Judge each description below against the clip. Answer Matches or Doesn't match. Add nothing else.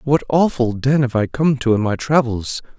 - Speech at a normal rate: Doesn't match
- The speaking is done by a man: Matches